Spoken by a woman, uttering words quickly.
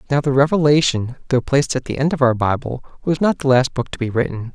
No: male; fast, 250 wpm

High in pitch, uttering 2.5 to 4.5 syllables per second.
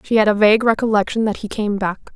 No: high, 210 Hz; 6.4 syllables/s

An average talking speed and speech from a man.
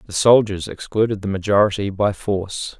Yes: average, 150 wpm; male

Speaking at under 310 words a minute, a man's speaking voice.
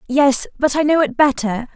No: fast, 205 wpm; female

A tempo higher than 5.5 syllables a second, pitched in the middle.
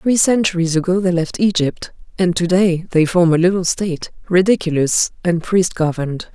No: 5.1 syllables/s; medium, 175 Hz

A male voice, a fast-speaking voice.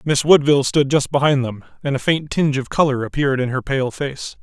Yes: male; fast, 230 wpm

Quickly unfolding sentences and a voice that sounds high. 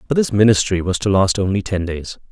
No: fast, 235 wpm; low, 100 Hz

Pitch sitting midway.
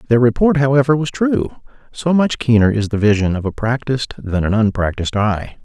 No: low, 120 Hz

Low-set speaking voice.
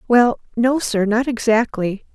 No: high, 230 Hz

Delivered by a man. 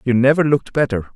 Yes: male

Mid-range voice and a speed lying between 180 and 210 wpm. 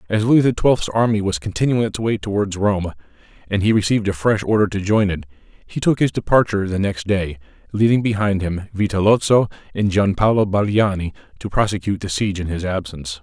No: low, 100 Hz; average, 190 wpm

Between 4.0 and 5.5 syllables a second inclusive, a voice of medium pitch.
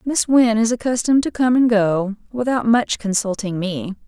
No: 4.8 syllables/s; high, 225 Hz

